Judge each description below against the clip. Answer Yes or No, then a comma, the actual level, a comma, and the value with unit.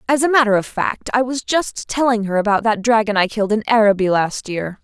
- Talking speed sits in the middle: No, fast, 235 wpm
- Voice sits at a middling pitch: No, high, 220 Hz